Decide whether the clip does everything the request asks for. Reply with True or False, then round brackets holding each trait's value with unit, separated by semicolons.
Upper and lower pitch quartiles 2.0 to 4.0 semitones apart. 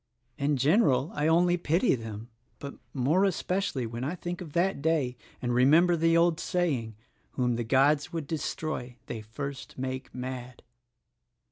False (5.0 semitones)